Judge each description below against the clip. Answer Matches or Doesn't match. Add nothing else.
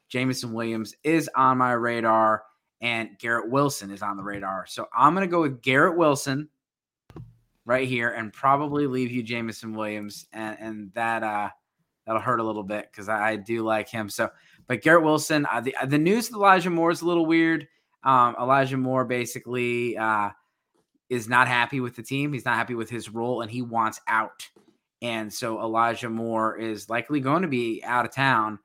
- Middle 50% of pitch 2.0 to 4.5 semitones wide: Matches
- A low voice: Matches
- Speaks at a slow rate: Doesn't match